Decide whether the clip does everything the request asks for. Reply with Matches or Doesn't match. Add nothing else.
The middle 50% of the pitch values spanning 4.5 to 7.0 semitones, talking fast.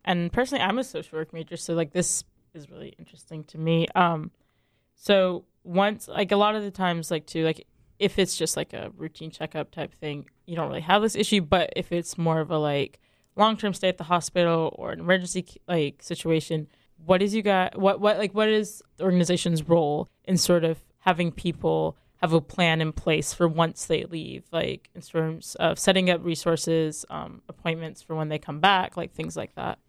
Doesn't match